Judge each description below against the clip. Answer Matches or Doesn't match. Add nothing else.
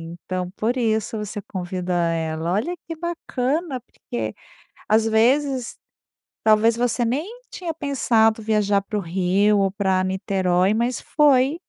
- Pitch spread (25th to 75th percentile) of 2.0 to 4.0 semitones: Doesn't match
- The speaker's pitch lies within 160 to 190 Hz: Doesn't match